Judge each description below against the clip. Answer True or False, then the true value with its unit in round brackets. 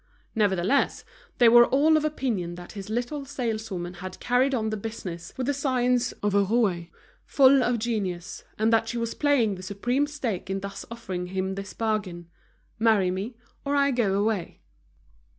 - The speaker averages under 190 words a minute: True (170 wpm)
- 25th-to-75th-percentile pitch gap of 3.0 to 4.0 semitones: False (4.5 semitones)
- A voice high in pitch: True (220 Hz)